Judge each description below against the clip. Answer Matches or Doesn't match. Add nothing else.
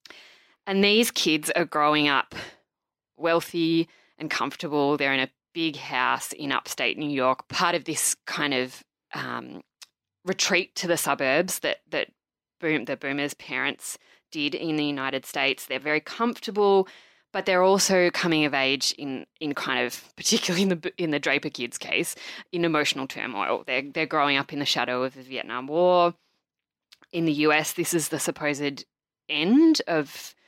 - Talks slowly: Doesn't match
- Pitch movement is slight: Doesn't match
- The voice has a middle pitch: Matches